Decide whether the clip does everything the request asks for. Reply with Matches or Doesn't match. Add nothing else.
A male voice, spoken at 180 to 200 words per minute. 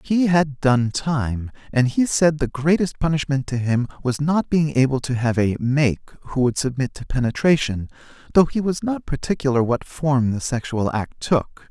Matches